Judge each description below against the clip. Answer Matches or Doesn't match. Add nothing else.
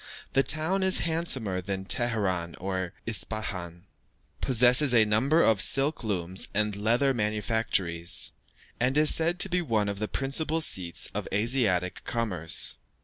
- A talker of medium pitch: Doesn't match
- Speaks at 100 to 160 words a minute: Matches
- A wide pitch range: Matches